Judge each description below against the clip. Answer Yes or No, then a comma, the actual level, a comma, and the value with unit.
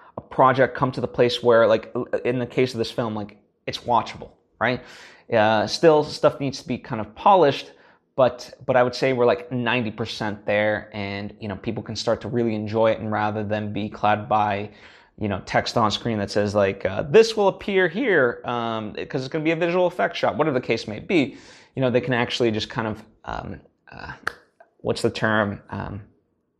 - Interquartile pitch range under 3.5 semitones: Yes, average, 3.0 semitones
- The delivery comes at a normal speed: No, fast, 215 wpm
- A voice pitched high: No, low, 115 Hz